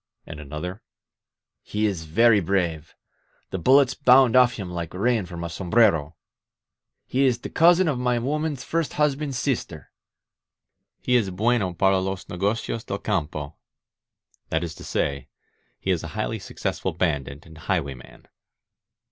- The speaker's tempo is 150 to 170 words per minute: Yes, average, 155 wpm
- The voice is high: No, very low, 95 Hz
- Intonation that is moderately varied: No, wide, 7.1 semitones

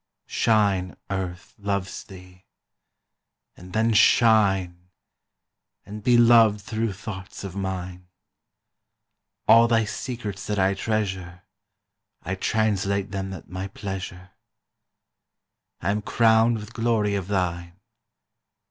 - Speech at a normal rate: No, slow, 105 wpm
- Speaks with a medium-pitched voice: No, low, 100 Hz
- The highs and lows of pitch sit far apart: No, average, 2.8 semitones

